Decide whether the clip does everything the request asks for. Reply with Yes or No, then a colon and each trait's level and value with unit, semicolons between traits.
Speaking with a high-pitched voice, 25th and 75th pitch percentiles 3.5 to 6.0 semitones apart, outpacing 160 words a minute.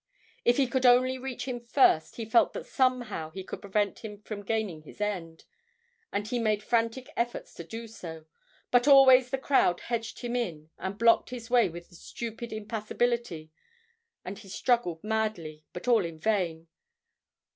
Yes: high, 220 Hz; average, 5.1 semitones; average, 170 wpm